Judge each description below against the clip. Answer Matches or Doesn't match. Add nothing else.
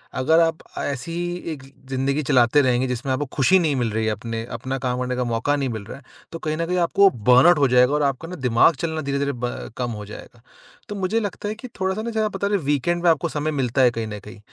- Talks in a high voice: Doesn't match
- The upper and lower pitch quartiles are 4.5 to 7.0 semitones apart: Matches